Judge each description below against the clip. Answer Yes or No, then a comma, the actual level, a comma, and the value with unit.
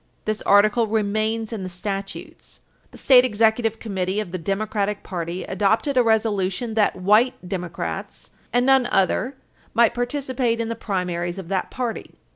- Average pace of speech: Yes, average, 150 wpm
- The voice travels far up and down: No, average, 3.2 semitones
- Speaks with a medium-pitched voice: No, high, 215 Hz